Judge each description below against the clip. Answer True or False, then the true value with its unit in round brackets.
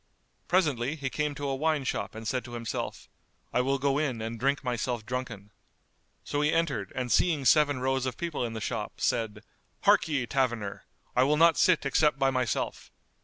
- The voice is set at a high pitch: False (130 Hz)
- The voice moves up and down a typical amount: True (3.6 semitones)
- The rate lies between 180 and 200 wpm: True (185 wpm)